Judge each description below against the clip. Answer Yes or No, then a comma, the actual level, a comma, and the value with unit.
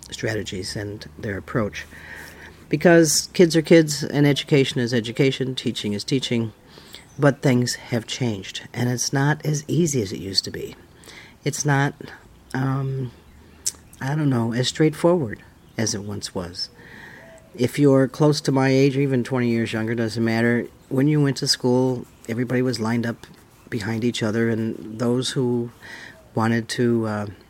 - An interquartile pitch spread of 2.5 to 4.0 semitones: Yes, average, 3.6 semitones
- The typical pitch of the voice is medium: No, low, 120 Hz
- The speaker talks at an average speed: Yes, average, 155 wpm